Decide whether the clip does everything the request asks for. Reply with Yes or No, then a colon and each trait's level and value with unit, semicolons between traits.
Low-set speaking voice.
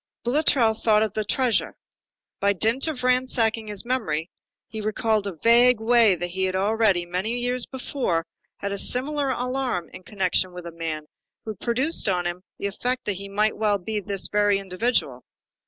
No: high, 215 Hz